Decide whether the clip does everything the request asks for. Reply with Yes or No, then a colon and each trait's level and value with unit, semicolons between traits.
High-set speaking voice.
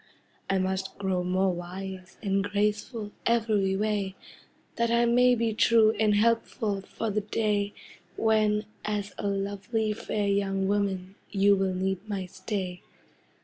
Yes: high, 200 Hz